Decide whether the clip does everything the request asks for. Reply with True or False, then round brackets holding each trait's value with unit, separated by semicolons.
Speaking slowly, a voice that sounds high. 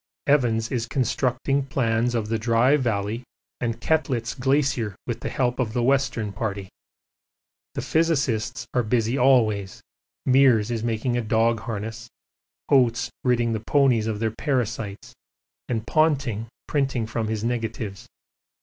False (130 wpm; 115 Hz)